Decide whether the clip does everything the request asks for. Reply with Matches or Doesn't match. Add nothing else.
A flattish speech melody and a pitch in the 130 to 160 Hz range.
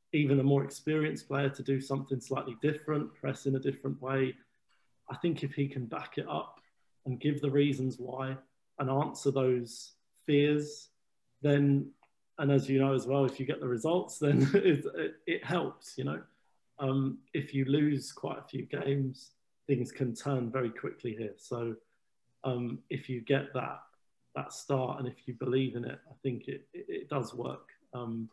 Matches